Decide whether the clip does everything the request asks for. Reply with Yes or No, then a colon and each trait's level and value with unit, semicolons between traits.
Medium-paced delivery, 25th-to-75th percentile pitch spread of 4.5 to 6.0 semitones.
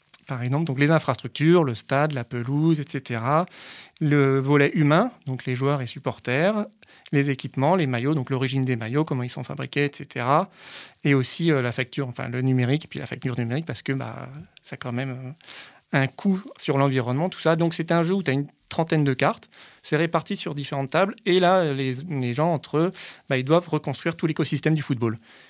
No: average, 205 wpm; average, 3.6 semitones